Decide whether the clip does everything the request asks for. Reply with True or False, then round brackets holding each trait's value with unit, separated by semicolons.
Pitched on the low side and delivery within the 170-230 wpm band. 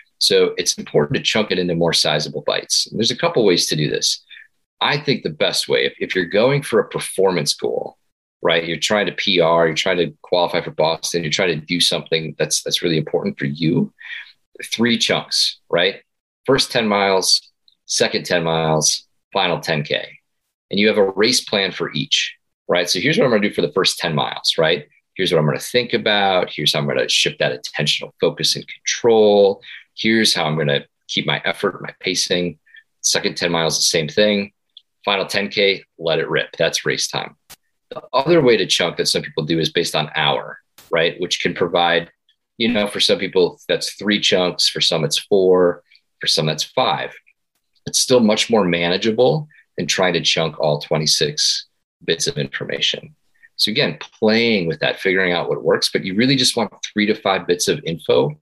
True (110 Hz; 200 wpm)